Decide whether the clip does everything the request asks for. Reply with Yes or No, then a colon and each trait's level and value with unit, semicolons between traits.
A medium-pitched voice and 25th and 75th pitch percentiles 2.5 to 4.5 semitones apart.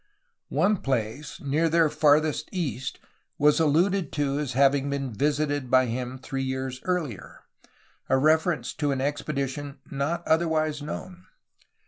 Yes: medium, 145 Hz; average, 2.9 semitones